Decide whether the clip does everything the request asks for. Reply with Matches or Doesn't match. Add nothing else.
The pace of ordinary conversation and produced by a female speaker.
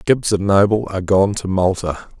Doesn't match